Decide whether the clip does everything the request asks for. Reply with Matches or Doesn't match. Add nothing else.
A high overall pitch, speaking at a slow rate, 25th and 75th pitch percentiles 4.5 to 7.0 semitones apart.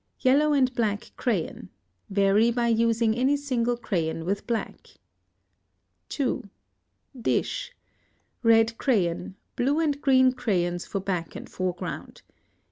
Matches